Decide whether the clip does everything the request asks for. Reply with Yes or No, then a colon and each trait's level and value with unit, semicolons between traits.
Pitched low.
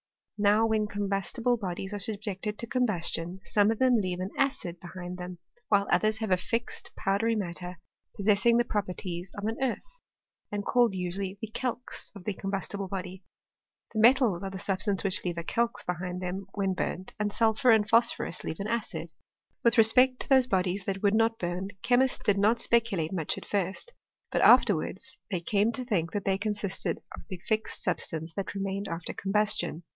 No: high, 200 Hz